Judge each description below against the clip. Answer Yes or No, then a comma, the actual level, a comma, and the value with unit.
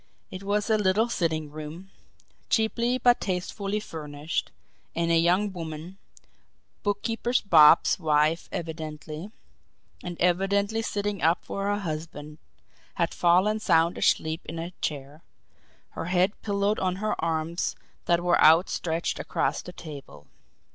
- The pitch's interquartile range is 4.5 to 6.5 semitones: No, average, 4.0 semitones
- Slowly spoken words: Yes, slow, 125 wpm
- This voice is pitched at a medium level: Yes, medium, 175 Hz